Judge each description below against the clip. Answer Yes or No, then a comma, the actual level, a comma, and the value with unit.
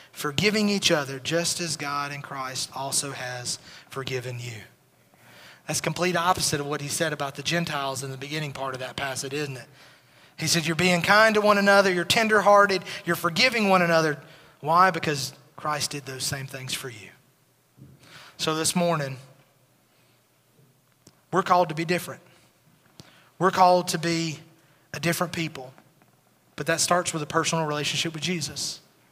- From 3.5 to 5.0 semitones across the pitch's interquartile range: Yes, average, 3.8 semitones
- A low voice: No, medium, 155 Hz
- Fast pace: No, average, 160 wpm